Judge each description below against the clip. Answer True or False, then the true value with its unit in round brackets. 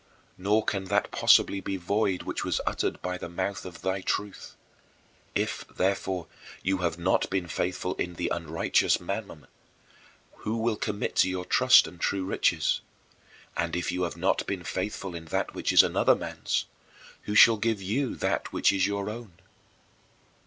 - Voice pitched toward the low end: True (95 Hz)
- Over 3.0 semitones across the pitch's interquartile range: False (2.5 semitones)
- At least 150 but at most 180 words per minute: True (170 wpm)